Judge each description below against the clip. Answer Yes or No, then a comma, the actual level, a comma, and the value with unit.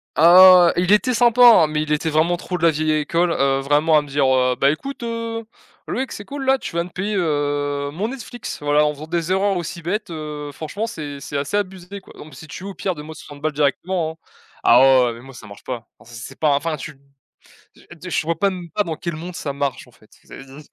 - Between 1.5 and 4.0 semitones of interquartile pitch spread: No, average, 4.5 semitones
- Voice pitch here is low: No, medium, 160 Hz